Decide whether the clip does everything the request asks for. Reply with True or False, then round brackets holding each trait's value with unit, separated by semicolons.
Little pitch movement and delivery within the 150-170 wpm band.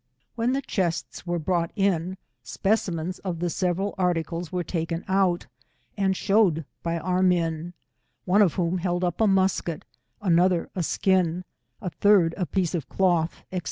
True (2.3 semitones; 160 wpm)